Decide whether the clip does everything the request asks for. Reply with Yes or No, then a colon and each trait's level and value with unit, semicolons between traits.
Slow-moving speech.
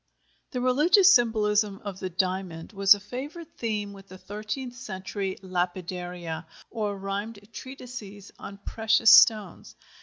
Yes: slow, 125 wpm